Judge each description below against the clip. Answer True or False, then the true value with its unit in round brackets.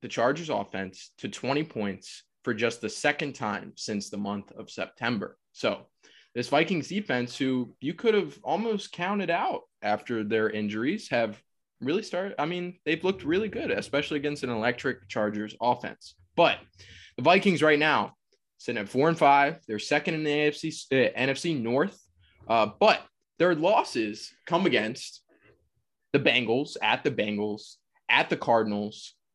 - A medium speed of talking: True (155 wpm)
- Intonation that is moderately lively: False (6.6 semitones)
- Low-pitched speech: True (130 Hz)